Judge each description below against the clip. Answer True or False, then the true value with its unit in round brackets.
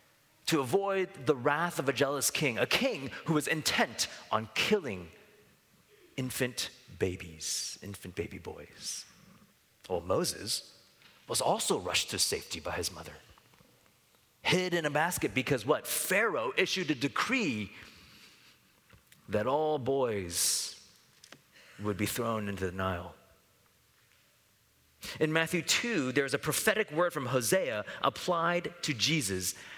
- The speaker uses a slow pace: True (125 wpm)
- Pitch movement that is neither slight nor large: False (7.5 semitones)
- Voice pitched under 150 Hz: True (140 Hz)